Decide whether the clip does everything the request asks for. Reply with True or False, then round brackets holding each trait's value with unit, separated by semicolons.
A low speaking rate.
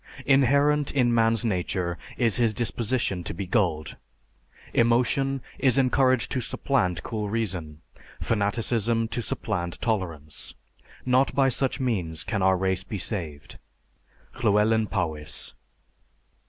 True (115 wpm)